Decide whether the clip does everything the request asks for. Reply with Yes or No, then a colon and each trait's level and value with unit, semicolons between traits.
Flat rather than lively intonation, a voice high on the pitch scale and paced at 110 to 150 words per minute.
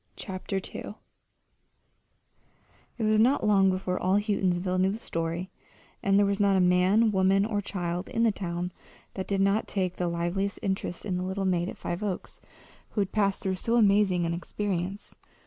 No: narrow, 2.1 semitones; high, 195 Hz; average, 180 wpm